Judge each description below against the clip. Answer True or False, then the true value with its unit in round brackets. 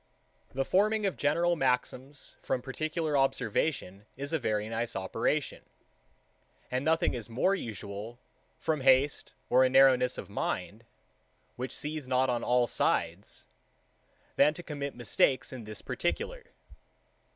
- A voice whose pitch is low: True (130 Hz)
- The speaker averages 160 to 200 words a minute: False (135 wpm)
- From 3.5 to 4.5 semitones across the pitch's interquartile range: True (4.2 semitones)